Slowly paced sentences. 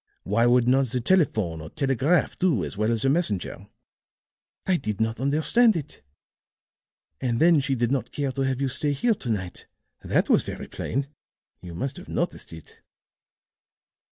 No: average, 170 wpm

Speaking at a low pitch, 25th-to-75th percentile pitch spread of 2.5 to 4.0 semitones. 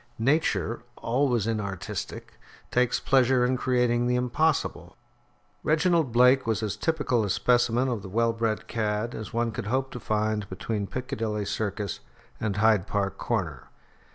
Yes: low, 115 Hz; average, 3.0 semitones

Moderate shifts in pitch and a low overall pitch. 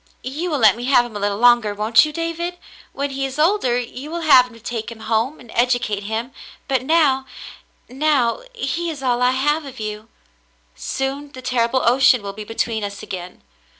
No: average, 4.1 semitones; very high, 250 Hz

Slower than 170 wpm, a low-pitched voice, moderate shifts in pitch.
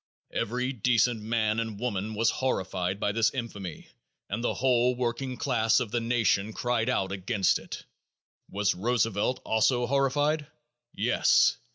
Yes: average, 140 wpm; low, 115 Hz; average, 3.2 semitones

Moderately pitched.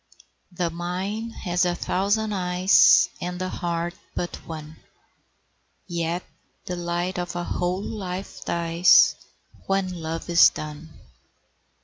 Yes: medium, 175 Hz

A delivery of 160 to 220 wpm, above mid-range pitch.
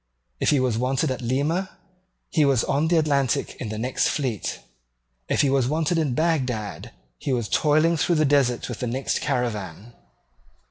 No: average, 175 wpm; low, 135 Hz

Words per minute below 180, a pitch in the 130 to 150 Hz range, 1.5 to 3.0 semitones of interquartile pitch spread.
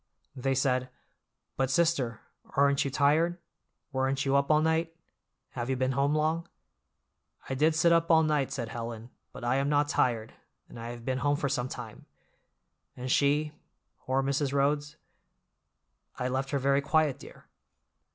Yes: average, 155 wpm; medium, 140 Hz; narrow, 2.6 semitones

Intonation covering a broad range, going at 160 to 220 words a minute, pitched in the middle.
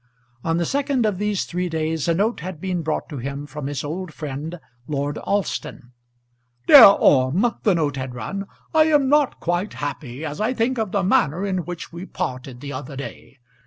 Yes: wide, 5.7 semitones; average, 195 wpm; medium, 170 Hz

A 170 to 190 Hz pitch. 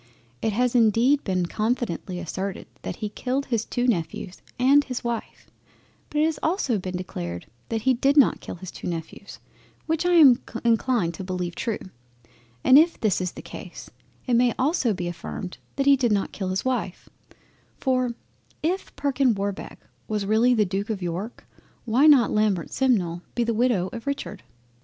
No: high, 230 Hz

